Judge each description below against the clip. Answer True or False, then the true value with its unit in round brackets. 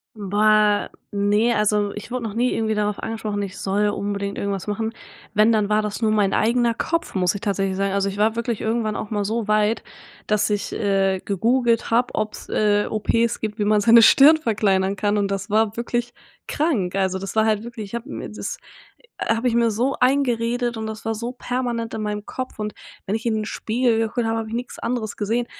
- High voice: True (215 Hz)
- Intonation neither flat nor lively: False (2.2 semitones)